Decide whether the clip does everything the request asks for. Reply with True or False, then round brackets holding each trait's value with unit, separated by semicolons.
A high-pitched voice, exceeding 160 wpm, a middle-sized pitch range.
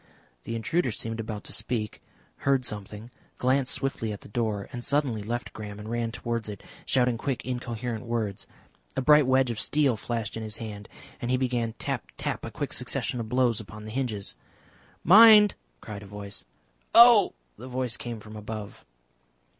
False (115 Hz; 175 wpm; 3.0 semitones)